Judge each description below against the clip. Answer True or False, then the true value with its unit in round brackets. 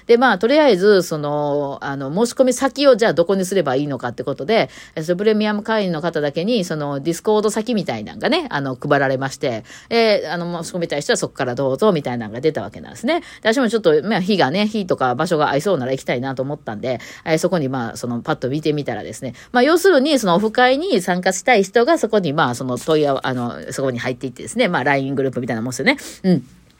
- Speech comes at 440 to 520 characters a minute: True (505 characters per minute)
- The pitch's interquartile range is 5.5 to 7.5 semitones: False (8.5 semitones)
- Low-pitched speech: False (170 Hz)